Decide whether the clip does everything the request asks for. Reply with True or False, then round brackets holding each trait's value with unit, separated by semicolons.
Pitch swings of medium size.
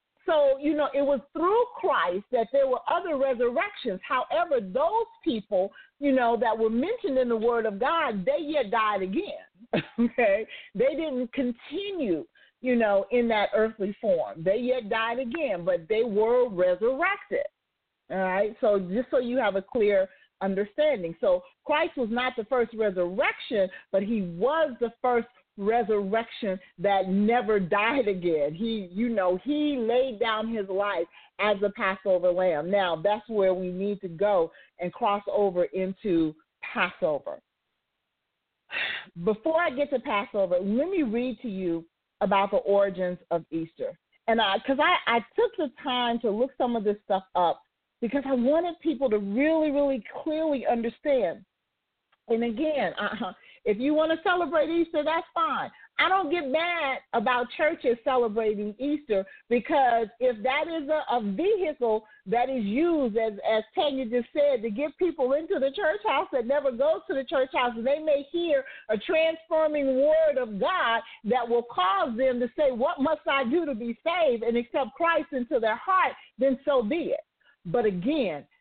False (5.9 semitones)